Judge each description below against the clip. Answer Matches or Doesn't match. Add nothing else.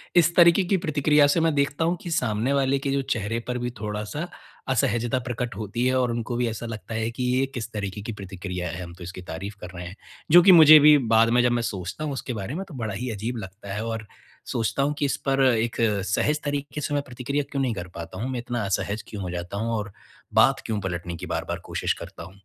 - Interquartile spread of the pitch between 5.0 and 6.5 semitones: Matches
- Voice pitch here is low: Matches